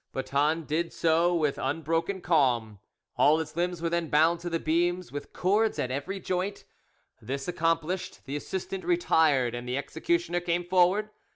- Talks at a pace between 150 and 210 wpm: Yes, average, 160 wpm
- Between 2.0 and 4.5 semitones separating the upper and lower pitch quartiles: Yes, average, 3.2 semitones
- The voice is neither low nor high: Yes, medium, 165 Hz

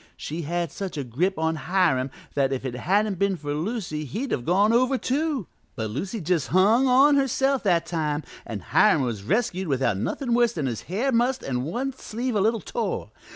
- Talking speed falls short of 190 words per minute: No, average, 200 wpm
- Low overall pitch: No, medium, 185 Hz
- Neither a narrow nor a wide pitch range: No, wide, 8.4 semitones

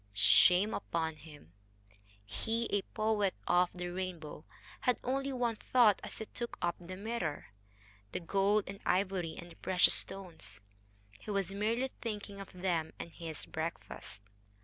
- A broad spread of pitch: No, average, 4.2 semitones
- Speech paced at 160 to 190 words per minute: No, average, 150 wpm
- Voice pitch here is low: No, high, 190 Hz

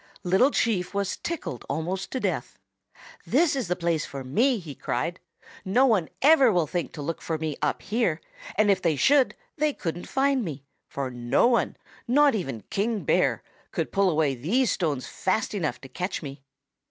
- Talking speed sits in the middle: Yes, average, 180 wpm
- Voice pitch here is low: No, medium, 185 Hz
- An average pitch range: No, wide, 7.3 semitones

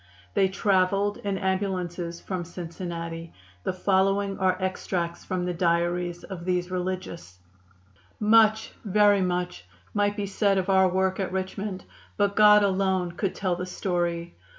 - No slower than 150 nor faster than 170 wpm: No, average, 140 wpm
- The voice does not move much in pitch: Yes, narrow, 1.9 semitones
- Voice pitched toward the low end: No, medium, 185 Hz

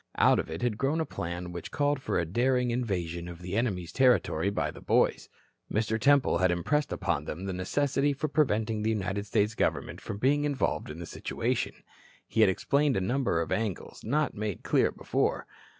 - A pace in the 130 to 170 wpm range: No, average, 195 wpm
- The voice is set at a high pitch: No, low, 110 Hz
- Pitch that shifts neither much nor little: No, wide, 6.8 semitones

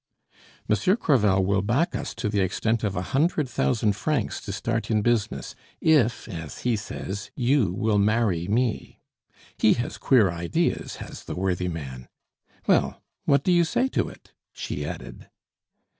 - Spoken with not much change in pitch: No, average, 4.6 semitones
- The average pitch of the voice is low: Yes, low, 110 Hz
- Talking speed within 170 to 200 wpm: No, average, 160 wpm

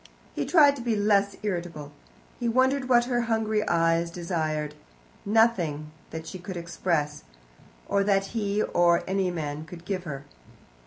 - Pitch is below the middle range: No, medium, 185 Hz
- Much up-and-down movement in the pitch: No, average, 4.8 semitones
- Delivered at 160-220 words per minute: No, average, 150 wpm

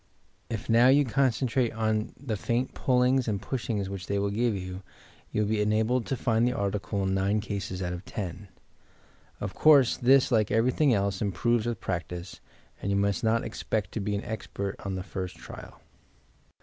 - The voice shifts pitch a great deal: No, average, 3.4 semitones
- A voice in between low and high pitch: No, low, 110 Hz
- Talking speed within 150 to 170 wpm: No, average, 185 wpm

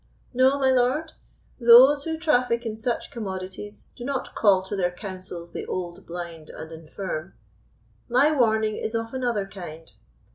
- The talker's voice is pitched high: Yes, high, 220 Hz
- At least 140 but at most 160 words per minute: Yes, average, 150 wpm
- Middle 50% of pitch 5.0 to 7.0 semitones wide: Yes, wide, 5.4 semitones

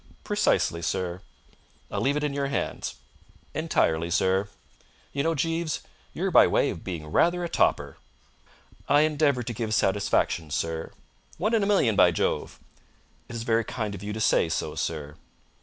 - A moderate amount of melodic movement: No, wide, 9.0 semitones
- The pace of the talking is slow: No, average, 165 wpm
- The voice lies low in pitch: Yes, low, 110 Hz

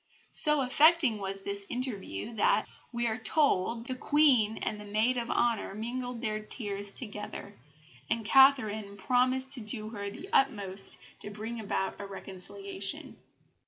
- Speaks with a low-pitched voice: No, high, 220 Hz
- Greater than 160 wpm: No, average, 140 wpm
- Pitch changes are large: No, average, 3.9 semitones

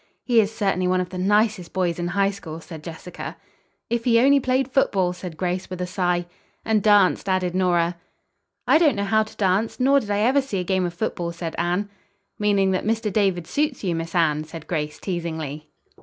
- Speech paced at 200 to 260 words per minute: Yes, fast, 205 wpm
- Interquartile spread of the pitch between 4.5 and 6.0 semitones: No, average, 3.7 semitones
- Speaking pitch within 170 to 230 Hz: Yes, medium, 185 Hz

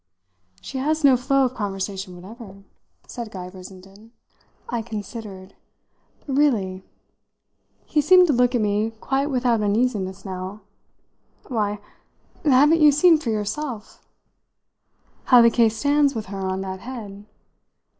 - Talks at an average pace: No, slow, 130 wpm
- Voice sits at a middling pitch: No, high, 225 Hz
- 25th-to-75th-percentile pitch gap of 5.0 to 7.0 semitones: Yes, average, 5.3 semitones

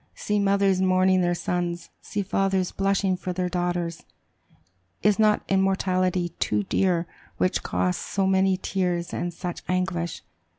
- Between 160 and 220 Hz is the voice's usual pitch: Yes, medium, 185 Hz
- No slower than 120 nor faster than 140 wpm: Yes, slow, 135 wpm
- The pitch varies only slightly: Yes, narrow, 1.6 semitones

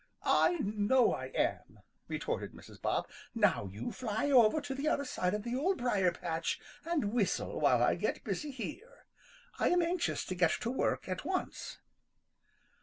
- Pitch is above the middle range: Yes, high, 245 Hz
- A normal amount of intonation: No, wide, 7.6 semitones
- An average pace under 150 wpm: No, average, 170 wpm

